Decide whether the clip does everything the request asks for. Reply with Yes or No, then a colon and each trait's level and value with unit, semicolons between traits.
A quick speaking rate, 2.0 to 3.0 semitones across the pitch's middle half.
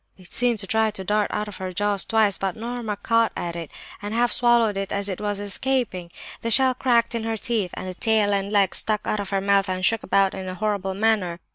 Yes: fast, 245 wpm; narrow, 2.6 semitones